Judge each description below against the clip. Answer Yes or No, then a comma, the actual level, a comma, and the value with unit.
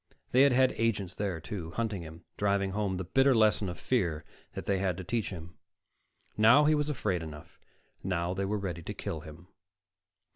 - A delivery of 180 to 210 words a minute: Yes, average, 185 wpm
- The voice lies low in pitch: Yes, low, 100 Hz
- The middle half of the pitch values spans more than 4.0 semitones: Yes, average, 4.5 semitones